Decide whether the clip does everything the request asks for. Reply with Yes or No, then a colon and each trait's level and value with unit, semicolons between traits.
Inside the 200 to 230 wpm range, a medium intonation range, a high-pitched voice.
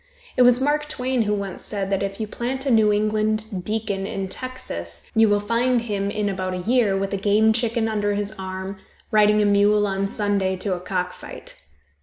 No: fast, 205 wpm; narrow, 2.3 semitones; high, 205 Hz